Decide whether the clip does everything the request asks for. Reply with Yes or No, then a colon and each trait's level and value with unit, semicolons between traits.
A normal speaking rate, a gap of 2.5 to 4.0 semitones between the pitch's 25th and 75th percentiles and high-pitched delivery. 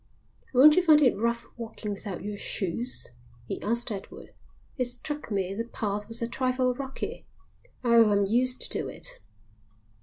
Yes: average, 155 wpm; average, 3.5 semitones; high, 235 Hz